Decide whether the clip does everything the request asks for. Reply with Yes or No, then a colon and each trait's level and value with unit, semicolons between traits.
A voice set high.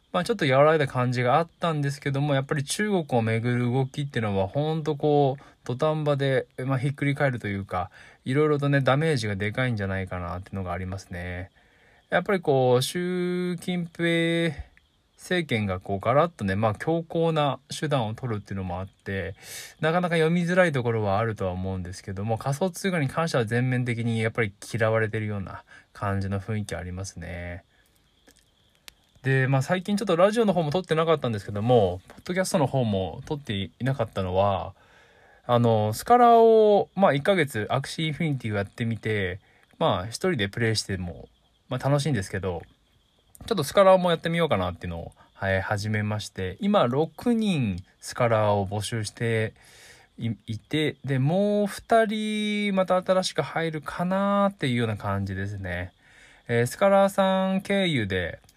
No: low, 125 Hz